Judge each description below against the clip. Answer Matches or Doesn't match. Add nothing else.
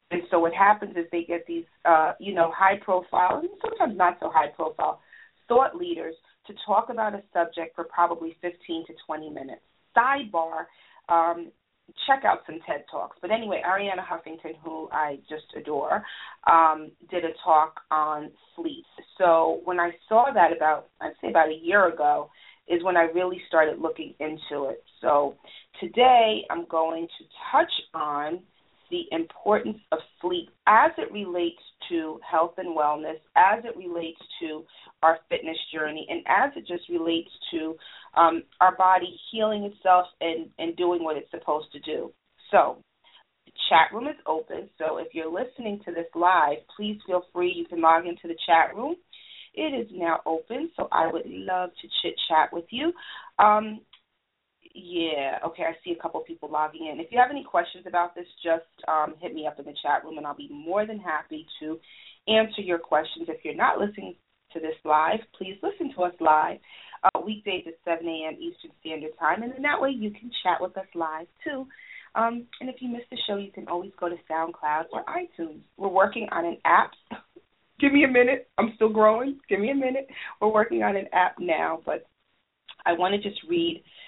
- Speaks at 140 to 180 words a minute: Doesn't match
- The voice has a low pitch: Doesn't match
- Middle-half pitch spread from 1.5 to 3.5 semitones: Doesn't match